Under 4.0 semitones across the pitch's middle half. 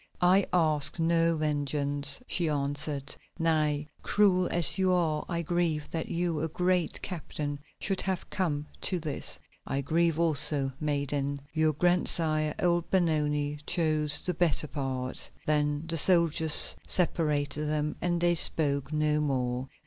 Yes: average, 2.7 semitones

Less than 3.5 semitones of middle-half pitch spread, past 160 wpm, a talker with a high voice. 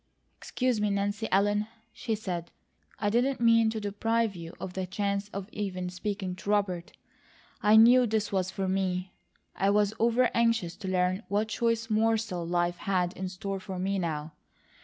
Yes: average, 3.1 semitones; average, 170 wpm; high, 200 Hz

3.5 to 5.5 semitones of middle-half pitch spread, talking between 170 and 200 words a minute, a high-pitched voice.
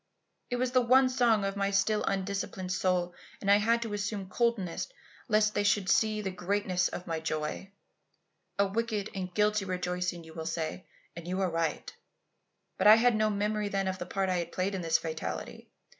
No: average, 2.8 semitones; average, 195 wpm; high, 195 Hz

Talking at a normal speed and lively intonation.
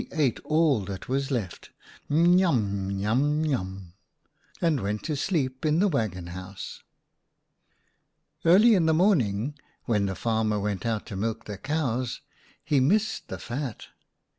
Yes: average, 165 wpm; wide, 7.3 semitones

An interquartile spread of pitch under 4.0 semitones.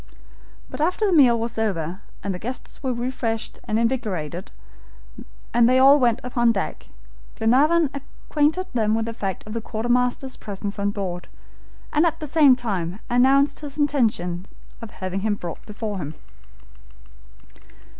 No: average, 4.8 semitones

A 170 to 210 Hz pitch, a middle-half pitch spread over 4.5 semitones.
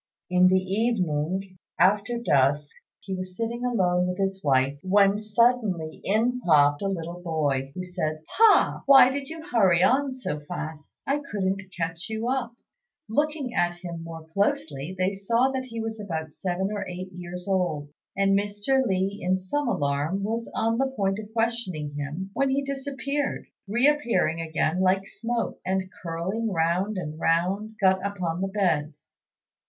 Yes: high, 190 Hz; average, 5.2 semitones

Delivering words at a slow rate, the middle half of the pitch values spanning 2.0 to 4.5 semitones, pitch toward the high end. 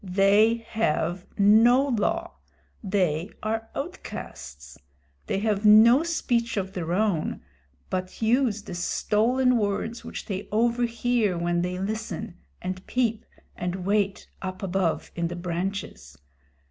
Yes: slow, 120 wpm; average, 4.0 semitones; high, 205 Hz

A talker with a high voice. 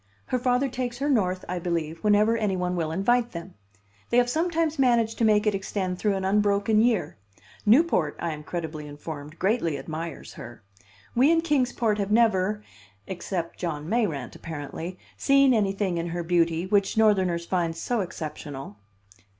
Yes: high, 195 Hz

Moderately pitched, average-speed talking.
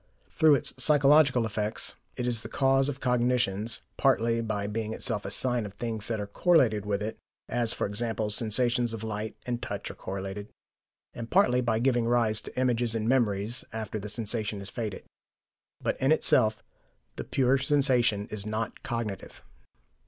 No: low, 115 Hz; average, 165 wpm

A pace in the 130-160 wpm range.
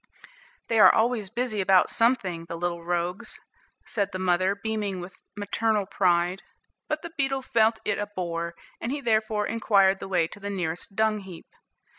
No: average, 170 wpm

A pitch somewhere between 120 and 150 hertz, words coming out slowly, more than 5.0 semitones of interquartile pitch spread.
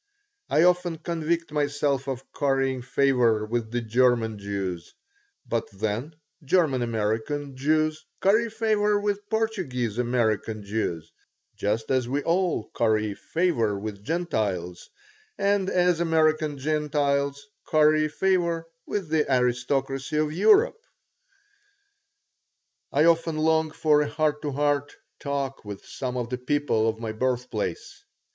Yes: medium, 140 Hz; slow, 125 wpm; wide, 5.6 semitones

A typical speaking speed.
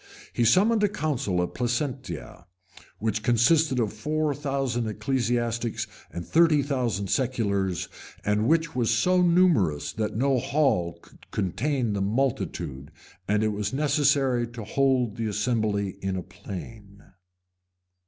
No: slow, 130 wpm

